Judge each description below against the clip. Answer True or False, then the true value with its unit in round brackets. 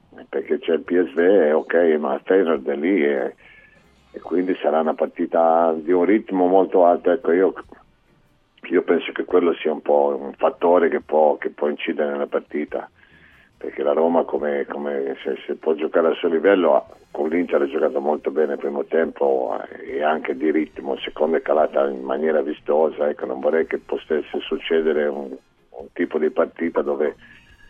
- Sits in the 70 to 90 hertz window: True (80 Hz)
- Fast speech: True (175 wpm)